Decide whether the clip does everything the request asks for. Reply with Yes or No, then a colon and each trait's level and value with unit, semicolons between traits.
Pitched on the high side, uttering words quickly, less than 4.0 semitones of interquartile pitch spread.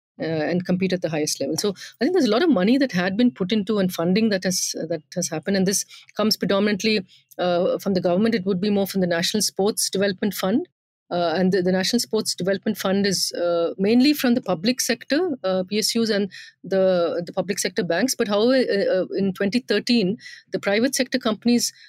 Yes: high, 200 Hz; fast, 215 wpm; average, 3.6 semitones